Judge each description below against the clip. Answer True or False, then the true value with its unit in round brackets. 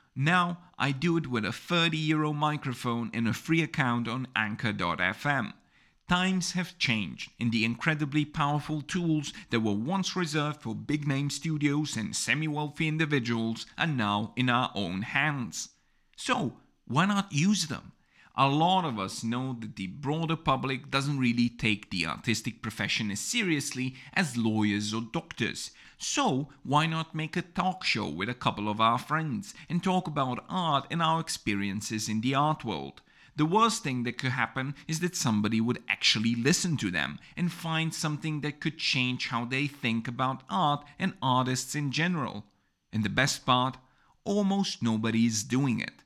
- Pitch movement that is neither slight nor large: False (5.7 semitones)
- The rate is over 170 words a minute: False (165 wpm)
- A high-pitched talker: False (135 Hz)